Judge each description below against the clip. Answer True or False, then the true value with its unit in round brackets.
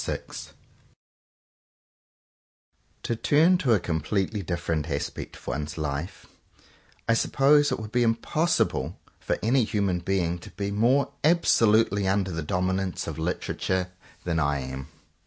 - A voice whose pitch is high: False (95 Hz)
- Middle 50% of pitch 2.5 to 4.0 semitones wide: False (5.6 semitones)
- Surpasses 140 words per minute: False (135 wpm)